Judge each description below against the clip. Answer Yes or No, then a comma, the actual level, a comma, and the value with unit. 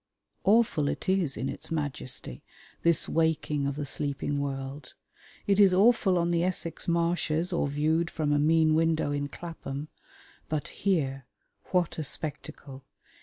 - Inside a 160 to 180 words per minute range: No, average, 145 wpm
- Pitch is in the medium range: Yes, medium, 155 Hz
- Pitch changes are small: No, average, 3.2 semitones